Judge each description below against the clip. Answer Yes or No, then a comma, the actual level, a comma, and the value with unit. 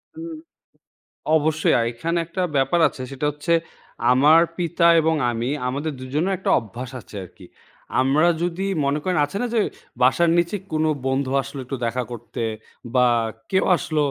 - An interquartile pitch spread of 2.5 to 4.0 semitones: No, average, 4.7 semitones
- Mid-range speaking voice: Yes, medium, 150 Hz